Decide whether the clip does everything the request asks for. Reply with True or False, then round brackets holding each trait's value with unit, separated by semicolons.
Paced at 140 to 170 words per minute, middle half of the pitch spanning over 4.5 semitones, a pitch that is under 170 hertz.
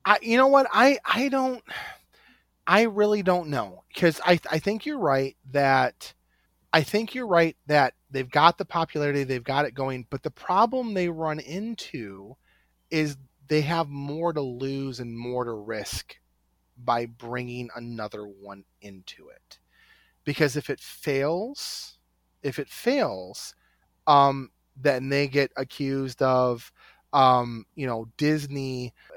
True (145 wpm; 5.3 semitones; 140 Hz)